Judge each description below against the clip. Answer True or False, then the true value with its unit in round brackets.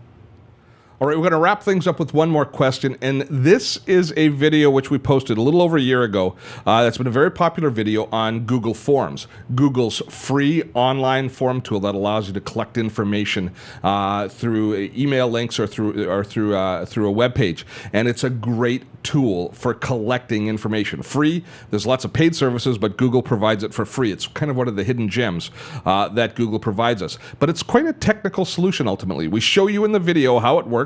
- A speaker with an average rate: False (210 wpm)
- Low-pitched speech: True (125 Hz)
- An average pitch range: True (4.7 semitones)